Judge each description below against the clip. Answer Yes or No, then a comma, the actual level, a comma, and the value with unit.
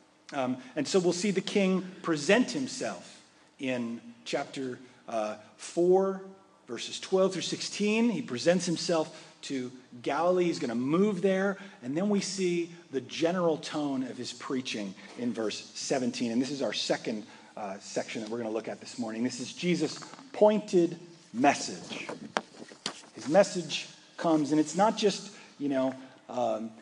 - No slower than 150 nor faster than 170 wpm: Yes, average, 155 wpm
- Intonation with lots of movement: Yes, wide, 6.9 semitones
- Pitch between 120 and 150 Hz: No, medium, 165 Hz